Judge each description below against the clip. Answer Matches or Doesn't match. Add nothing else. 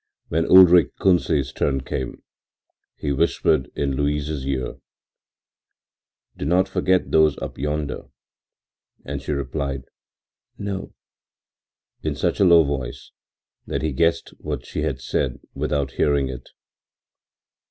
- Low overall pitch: Matches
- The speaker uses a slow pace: Matches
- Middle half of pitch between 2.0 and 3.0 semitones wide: Doesn't match